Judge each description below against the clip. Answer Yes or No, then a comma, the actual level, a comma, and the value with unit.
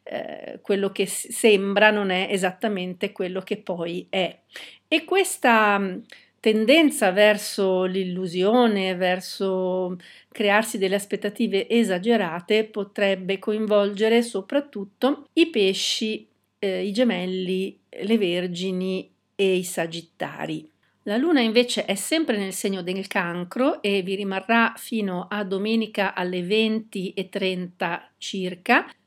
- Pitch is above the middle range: Yes, high, 200 Hz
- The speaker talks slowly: Yes, slow, 105 wpm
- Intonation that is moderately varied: Yes, average, 3.1 semitones